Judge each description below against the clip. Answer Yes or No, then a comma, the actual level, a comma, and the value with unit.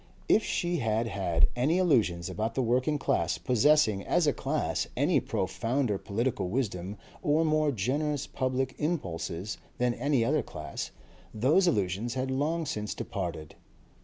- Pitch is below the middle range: Yes, low, 125 Hz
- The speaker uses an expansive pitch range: Yes, wide, 6.5 semitones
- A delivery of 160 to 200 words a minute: No, average, 140 wpm